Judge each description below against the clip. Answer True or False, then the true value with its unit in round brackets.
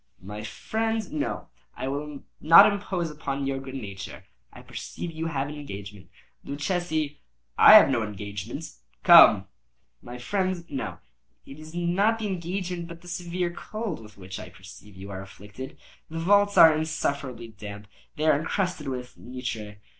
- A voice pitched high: False (140 Hz)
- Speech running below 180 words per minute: True (155 wpm)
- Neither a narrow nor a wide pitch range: False (8.2 semitones)